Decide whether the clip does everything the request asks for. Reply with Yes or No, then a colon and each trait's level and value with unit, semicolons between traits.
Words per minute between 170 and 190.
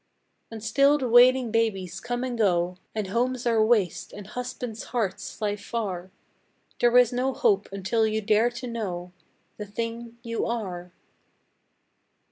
No: average, 145 wpm